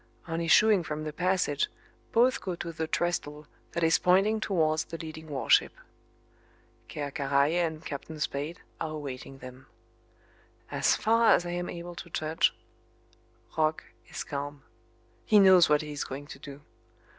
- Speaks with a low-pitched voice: No, medium, 160 Hz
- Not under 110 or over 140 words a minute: No, average, 155 wpm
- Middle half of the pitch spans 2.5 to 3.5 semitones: Yes, average, 3.2 semitones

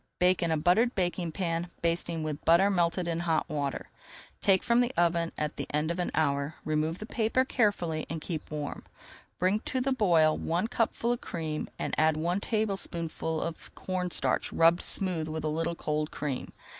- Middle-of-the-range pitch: Yes, medium, 170 Hz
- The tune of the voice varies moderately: Yes, average, 3.2 semitones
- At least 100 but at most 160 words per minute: No, average, 185 wpm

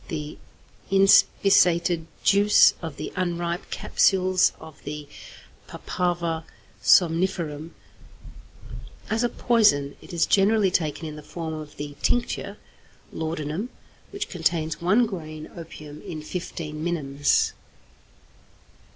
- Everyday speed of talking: No, slow, 110 wpm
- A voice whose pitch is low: No, medium, 170 Hz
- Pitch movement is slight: No, average, 3.4 semitones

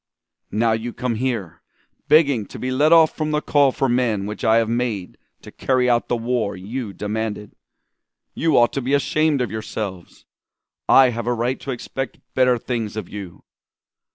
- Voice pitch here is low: Yes, low, 120 Hz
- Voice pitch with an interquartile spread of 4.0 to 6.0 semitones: No, average, 3.3 semitones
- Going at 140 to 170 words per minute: No, average, 180 wpm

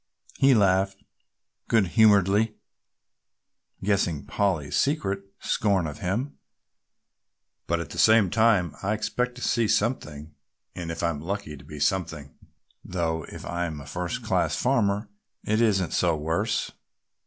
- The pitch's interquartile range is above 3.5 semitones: Yes, average, 4.5 semitones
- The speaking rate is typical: No, slow, 130 wpm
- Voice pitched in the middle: No, very low, 95 Hz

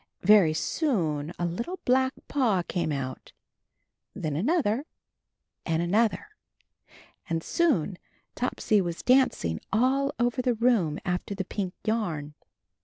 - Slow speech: Yes, slow, 120 wpm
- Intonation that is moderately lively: No, wide, 7.1 semitones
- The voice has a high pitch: Yes, high, 205 Hz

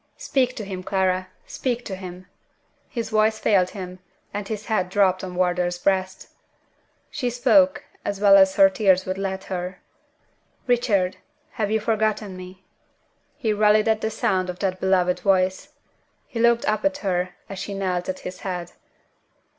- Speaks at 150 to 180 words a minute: Yes, average, 160 wpm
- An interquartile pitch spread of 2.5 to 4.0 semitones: Yes, average, 2.8 semitones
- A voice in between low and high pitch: No, high, 195 Hz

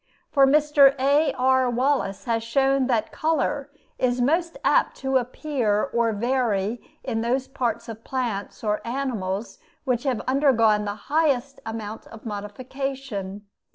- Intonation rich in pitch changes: No, average, 3.7 semitones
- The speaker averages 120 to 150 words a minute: Yes, slow, 135 wpm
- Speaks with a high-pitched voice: Yes, very high, 250 Hz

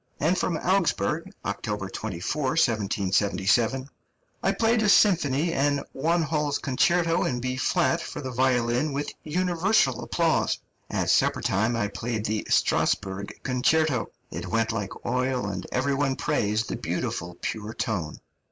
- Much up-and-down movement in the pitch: Yes, wide, 6.5 semitones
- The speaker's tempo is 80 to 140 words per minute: Yes, slow, 135 wpm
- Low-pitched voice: Yes, low, 130 Hz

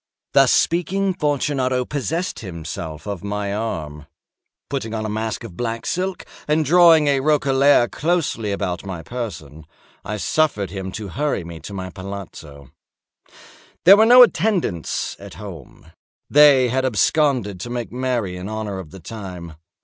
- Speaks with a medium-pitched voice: No, low, 110 Hz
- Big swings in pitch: Yes, wide, 7.5 semitones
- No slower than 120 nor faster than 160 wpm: Yes, average, 150 wpm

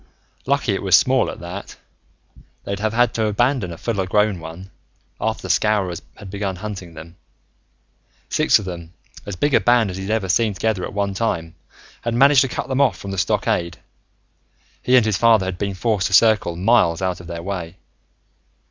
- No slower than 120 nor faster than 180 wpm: No, average, 190 wpm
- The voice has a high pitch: No, low, 100 Hz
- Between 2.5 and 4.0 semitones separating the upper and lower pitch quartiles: Yes, average, 3.7 semitones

